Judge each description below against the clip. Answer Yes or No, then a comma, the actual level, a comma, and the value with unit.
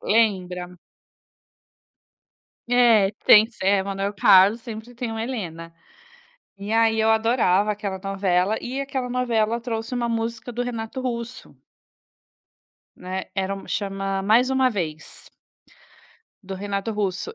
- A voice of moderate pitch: No, high, 215 Hz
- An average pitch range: Yes, average, 3.2 semitones